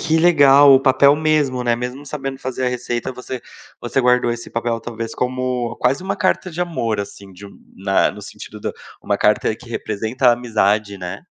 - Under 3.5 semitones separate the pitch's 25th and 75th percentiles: Yes, average, 2.9 semitones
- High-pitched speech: No, low, 125 Hz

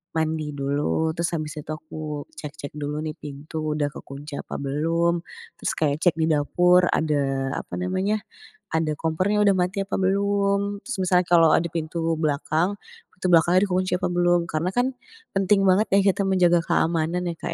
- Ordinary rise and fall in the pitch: Yes, average, 3.3 semitones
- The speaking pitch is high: No, medium, 165 Hz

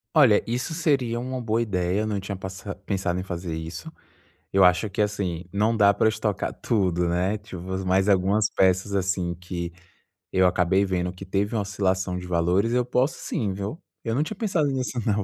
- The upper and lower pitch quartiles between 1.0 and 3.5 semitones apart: Yes, average, 3.2 semitones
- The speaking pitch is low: Yes, low, 100 Hz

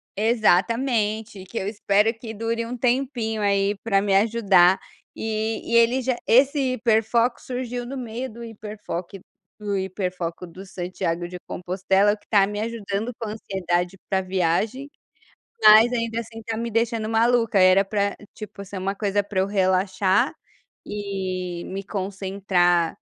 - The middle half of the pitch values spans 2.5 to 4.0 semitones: Yes, average, 3.2 semitones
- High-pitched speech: Yes, high, 210 Hz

